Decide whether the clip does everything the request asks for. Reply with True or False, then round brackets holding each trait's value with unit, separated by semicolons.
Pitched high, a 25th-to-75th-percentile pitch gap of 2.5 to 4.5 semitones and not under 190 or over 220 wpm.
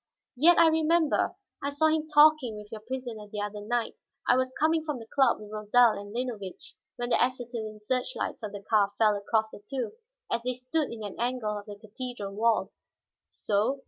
True (235 Hz; 3.8 semitones; 200 wpm)